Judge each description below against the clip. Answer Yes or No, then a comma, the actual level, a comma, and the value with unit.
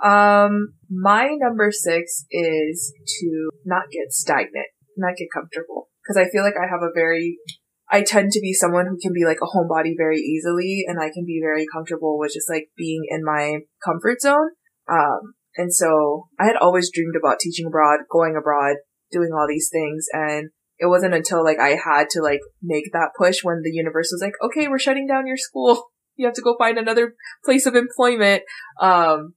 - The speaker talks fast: No, average, 195 wpm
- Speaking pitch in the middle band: Yes, medium, 170 Hz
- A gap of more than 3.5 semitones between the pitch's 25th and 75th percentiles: Yes, average, 4.5 semitones